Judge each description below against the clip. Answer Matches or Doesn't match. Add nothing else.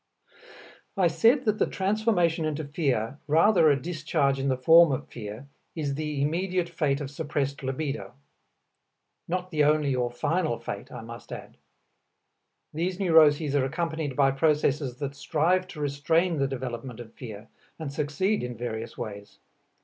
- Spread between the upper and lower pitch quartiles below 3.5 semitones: Doesn't match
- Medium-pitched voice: Matches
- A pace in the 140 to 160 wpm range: Matches